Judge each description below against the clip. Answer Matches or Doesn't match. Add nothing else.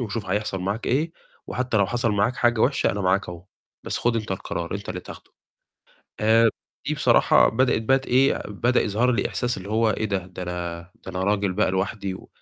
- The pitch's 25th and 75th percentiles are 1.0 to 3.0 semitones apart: Doesn't match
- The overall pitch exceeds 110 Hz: Doesn't match